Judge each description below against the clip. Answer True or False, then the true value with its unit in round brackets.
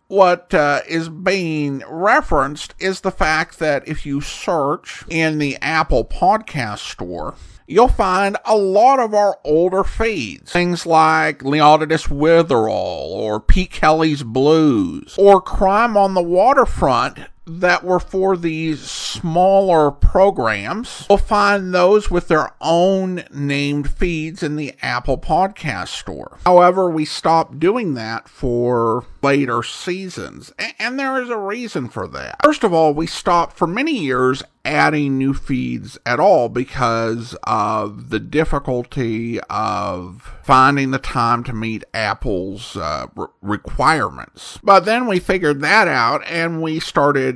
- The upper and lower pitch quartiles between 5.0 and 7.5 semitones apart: True (5.3 semitones)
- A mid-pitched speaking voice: True (160 Hz)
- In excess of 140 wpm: False (135 wpm)